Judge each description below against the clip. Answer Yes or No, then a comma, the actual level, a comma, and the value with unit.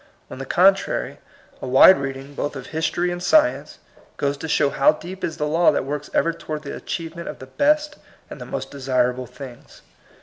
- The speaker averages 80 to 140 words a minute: No, average, 200 wpm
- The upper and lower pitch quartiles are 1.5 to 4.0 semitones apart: No, average, 4.5 semitones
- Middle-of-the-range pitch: Yes, medium, 150 Hz